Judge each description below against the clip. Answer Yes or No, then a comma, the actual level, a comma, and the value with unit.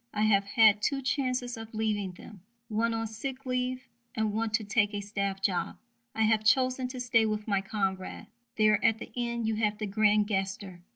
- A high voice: Yes, high, 215 Hz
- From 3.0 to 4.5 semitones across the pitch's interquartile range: No, narrow, 2.5 semitones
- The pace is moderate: Yes, average, 195 wpm